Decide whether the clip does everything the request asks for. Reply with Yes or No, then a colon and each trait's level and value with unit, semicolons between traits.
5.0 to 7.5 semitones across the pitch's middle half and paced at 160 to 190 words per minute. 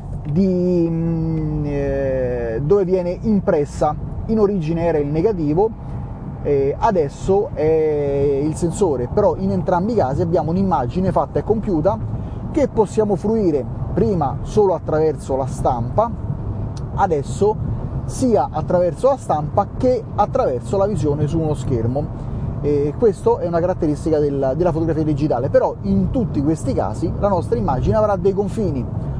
No: average, 5.3 semitones; average, 135 wpm